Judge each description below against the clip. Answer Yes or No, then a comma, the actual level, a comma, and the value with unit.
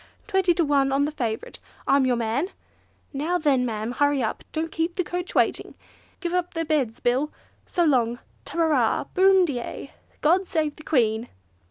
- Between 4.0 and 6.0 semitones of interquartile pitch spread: Yes, average, 5.3 semitones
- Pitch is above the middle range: Yes, very high, 290 Hz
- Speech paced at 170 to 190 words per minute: Yes, average, 185 wpm